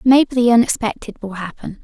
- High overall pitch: Yes, high, 230 Hz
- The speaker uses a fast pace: No, average, 165 wpm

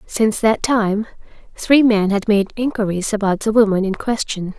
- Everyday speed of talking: Yes, average, 170 wpm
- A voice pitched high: Yes, high, 210 Hz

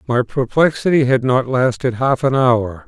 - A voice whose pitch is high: No, low, 130 Hz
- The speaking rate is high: No, average, 165 wpm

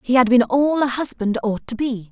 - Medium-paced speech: No, fast, 255 wpm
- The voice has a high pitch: Yes, high, 245 Hz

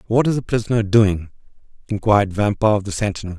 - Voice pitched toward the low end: Yes, low, 105 Hz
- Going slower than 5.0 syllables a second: No, 6.4 syllables/s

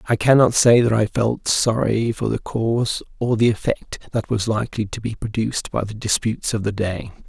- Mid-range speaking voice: No, low, 110 Hz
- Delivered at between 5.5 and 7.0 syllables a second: No, 5.3 syllables/s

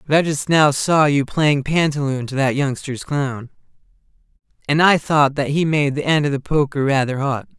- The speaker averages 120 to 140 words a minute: No, average, 200 wpm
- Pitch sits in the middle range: Yes, medium, 145 Hz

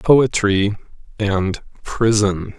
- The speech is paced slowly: Yes, slow, 70 wpm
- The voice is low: Yes, low, 105 Hz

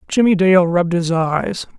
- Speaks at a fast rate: No, average, 170 wpm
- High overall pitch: No, medium, 180 Hz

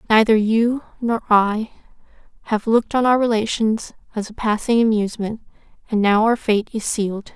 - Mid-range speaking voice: No, high, 220 Hz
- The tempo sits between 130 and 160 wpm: Yes, average, 155 wpm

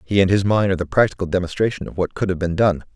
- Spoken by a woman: No, male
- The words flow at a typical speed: No, fast, 285 wpm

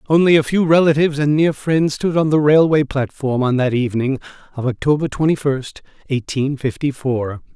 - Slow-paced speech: No, average, 175 wpm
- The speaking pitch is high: No, medium, 140 Hz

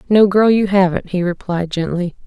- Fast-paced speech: No, average, 185 wpm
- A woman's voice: Yes, female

